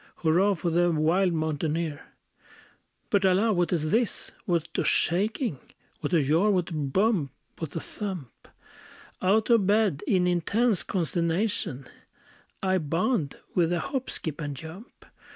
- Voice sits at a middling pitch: Yes, medium, 175 Hz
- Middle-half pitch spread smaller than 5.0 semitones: Yes, average, 4.1 semitones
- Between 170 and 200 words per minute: No, average, 140 wpm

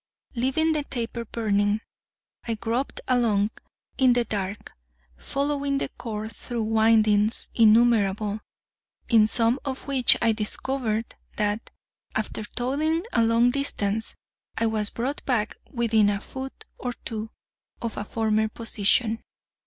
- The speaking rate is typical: No, slow, 125 wpm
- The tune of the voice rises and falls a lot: No, average, 2.7 semitones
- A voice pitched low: No, high, 225 Hz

